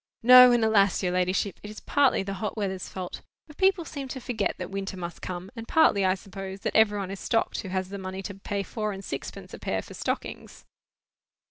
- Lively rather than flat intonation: No, average, 3.0 semitones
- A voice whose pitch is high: Yes, high, 200 Hz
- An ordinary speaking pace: No, fast, 225 wpm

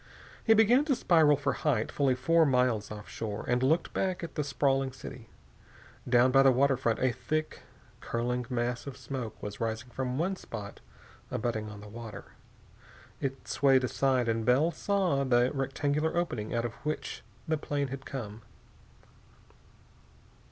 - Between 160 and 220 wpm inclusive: No, average, 150 wpm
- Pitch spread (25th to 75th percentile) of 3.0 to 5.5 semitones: Yes, average, 3.7 semitones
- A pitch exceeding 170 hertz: No, low, 130 Hz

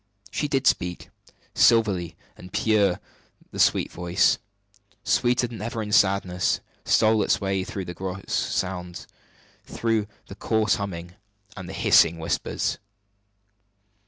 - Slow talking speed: Yes, slow, 125 wpm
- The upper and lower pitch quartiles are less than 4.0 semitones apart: Yes, average, 3.6 semitones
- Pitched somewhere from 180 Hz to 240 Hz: No, low, 100 Hz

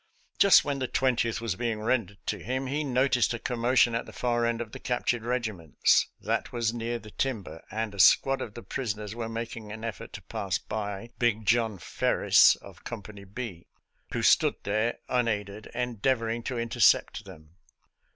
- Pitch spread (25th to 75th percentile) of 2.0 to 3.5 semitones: Yes, narrow, 2.4 semitones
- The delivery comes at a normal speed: Yes, average, 180 wpm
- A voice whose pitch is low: Yes, low, 115 Hz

